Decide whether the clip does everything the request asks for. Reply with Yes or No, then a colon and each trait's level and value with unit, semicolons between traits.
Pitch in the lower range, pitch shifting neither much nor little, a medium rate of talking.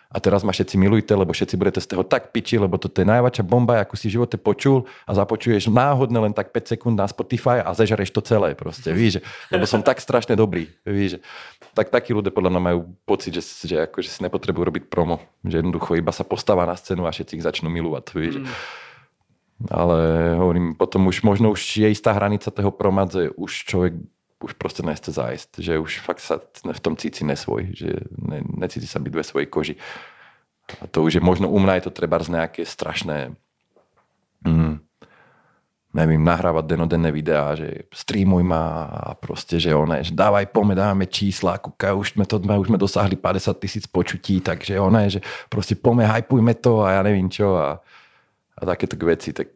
Yes: low, 100 Hz; average, 3.6 semitones; average, 195 wpm